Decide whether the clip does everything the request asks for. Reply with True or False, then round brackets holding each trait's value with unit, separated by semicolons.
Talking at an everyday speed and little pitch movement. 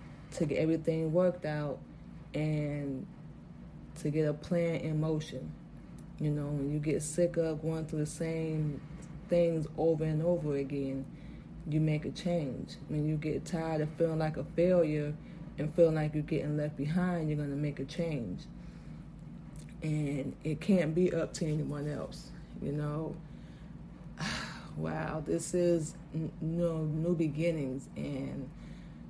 True (150 wpm; 1.9 semitones)